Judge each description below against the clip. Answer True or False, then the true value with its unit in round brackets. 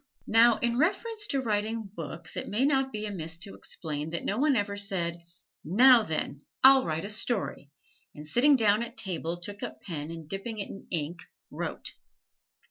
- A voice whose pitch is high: True (205 Hz)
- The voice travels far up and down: True (6.0 semitones)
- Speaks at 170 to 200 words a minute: True (180 wpm)